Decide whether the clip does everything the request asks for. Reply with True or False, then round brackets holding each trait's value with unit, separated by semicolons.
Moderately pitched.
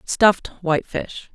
True (180 Hz)